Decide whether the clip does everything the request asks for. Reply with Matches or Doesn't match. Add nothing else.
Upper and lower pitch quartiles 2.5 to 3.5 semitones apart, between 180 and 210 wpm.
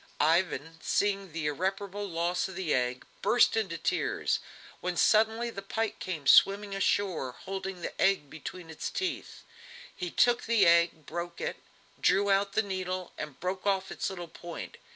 Doesn't match